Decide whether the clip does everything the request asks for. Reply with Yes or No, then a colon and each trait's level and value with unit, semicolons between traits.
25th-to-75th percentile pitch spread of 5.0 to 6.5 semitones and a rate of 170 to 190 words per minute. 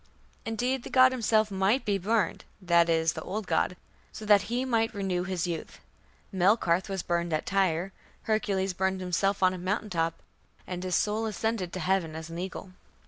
No: average, 3.4 semitones; average, 185 wpm